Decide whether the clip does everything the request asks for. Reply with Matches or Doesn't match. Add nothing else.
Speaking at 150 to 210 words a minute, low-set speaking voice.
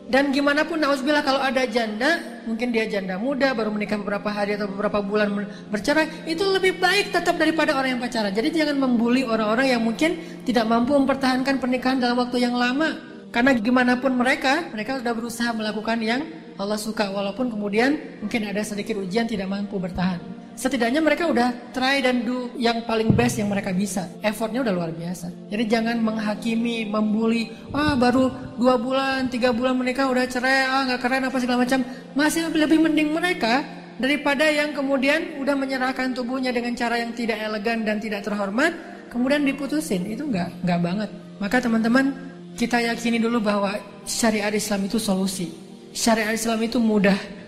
Doesn't match